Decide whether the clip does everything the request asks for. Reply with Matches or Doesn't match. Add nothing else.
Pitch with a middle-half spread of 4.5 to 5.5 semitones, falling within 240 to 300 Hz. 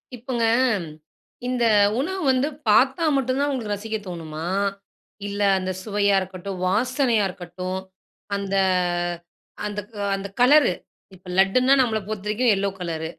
Doesn't match